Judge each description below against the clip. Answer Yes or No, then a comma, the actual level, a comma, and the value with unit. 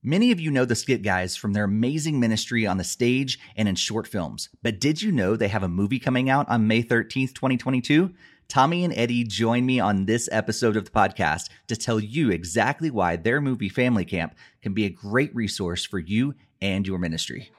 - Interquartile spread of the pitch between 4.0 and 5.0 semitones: Yes, average, 4.3 semitones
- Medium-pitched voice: No, low, 115 Hz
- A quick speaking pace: Yes, fast, 210 wpm